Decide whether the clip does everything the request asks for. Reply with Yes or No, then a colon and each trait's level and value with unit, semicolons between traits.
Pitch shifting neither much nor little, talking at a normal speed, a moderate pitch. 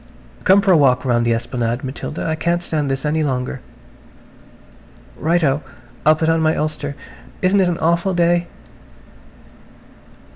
Yes: average, 4.1 semitones; average, 150 wpm; medium, 155 Hz